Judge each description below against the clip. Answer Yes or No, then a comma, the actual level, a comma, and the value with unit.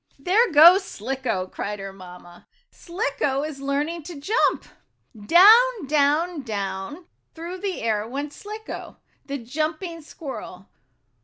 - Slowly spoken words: Yes, slow, 115 wpm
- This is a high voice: Yes, very high, 290 Hz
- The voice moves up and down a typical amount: No, wide, 7.6 semitones